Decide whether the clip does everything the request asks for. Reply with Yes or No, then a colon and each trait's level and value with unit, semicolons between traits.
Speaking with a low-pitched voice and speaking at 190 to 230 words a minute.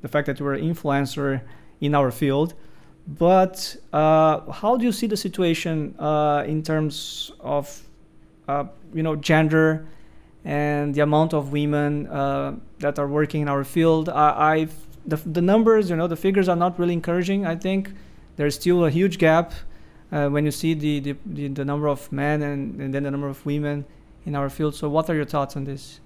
No: medium, 150 Hz; average, 195 wpm